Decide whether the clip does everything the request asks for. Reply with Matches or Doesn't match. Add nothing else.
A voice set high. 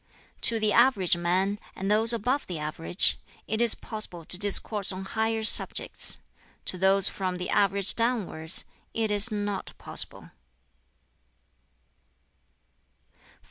Matches